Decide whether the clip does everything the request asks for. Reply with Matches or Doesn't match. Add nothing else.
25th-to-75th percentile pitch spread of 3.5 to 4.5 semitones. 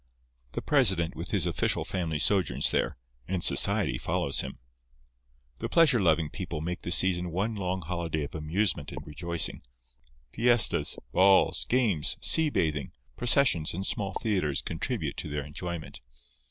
Matches